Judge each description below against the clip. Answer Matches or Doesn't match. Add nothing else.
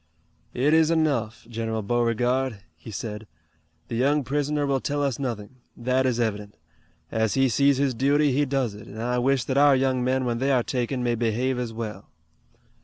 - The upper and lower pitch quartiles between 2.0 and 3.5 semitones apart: Matches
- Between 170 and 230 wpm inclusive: Matches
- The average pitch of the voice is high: Doesn't match